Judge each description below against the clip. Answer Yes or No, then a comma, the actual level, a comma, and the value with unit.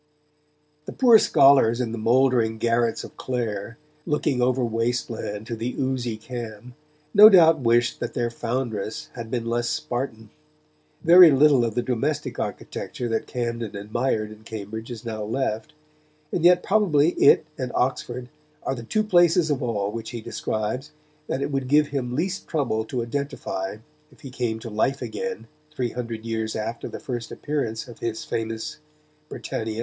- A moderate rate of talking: Yes, average, 165 wpm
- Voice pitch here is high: No, low, 120 Hz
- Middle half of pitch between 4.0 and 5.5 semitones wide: No, average, 3.5 semitones